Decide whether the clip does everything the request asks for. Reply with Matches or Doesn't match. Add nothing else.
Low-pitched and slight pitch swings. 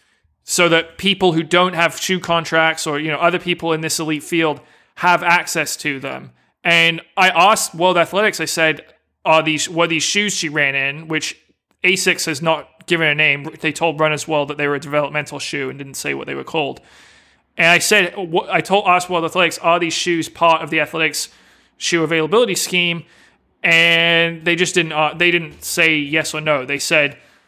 Doesn't match